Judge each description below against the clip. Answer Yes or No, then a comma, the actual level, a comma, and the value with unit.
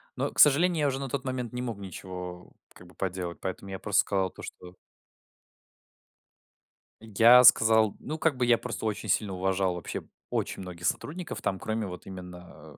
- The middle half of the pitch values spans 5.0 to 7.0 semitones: Yes, average, 5.3 semitones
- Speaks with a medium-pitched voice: No, low, 100 Hz